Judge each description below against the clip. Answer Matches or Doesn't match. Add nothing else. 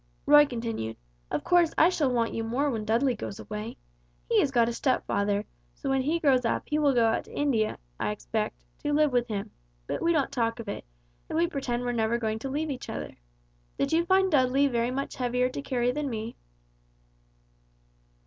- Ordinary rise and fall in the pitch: Matches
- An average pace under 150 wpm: Doesn't match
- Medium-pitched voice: Doesn't match